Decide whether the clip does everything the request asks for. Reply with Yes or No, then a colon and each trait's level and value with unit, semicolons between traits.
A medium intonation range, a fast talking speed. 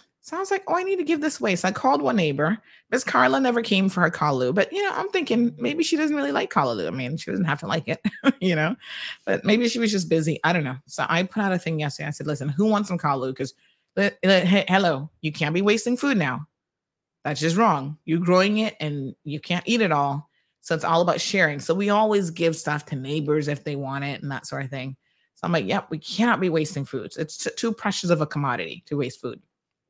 No: wide, 6.3 semitones; fast, 255 wpm